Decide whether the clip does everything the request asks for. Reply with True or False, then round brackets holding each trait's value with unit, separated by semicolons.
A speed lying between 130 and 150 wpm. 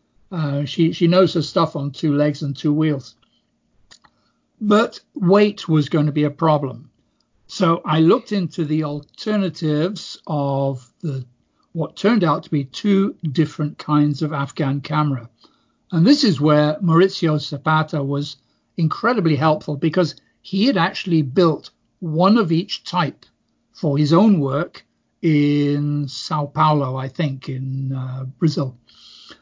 True (140 wpm)